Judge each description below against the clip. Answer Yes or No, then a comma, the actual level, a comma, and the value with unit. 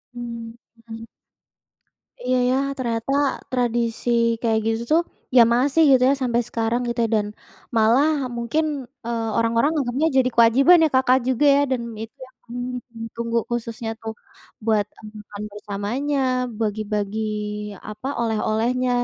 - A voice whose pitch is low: No, high, 235 Hz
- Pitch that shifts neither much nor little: No, narrow, 2.2 semitones